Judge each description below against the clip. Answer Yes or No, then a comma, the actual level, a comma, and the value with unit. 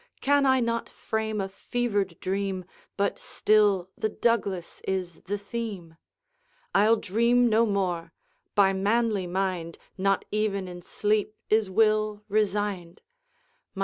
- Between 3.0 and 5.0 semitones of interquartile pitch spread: No, narrow, 2.5 semitones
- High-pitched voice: Yes, high, 205 Hz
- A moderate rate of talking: No, slow, 120 wpm